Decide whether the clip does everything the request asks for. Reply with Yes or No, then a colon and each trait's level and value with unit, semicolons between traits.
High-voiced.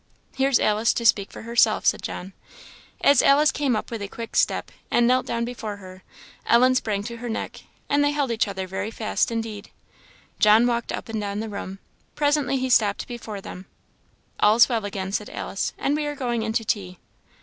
Yes: high, 225 Hz